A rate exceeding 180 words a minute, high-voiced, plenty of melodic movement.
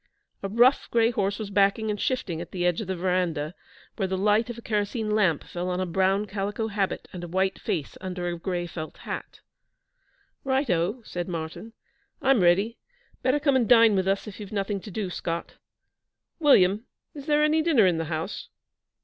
No: average, 195 wpm; high, 195 Hz; average, 4.0 semitones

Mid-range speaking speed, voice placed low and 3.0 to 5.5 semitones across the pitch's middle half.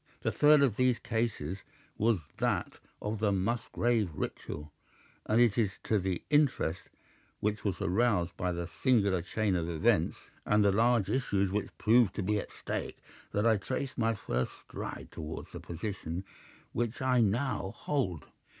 Yes: average, 160 wpm; low, 105 Hz; average, 4.3 semitones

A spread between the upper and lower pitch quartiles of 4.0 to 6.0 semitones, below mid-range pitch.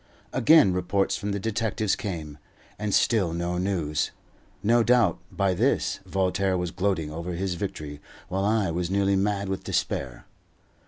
No: average, 2.7 semitones; very low, 95 Hz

